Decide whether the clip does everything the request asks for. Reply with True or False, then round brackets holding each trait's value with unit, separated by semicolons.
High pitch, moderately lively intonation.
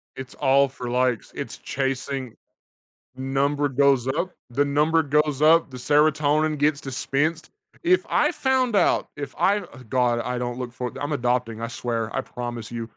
False (135 Hz; 3.3 semitones)